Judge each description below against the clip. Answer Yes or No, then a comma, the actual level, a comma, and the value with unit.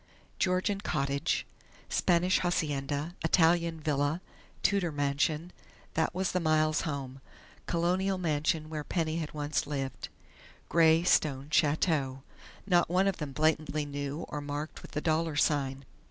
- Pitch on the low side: No, medium, 155 Hz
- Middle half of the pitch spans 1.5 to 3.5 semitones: Yes, average, 2.9 semitones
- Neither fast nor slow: No, slow, 130 wpm